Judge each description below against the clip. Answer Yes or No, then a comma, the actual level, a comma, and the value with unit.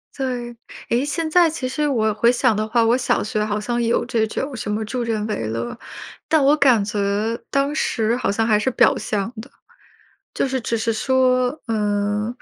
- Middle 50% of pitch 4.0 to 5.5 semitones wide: No, average, 3.4 semitones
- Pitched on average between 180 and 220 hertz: No, high, 235 Hz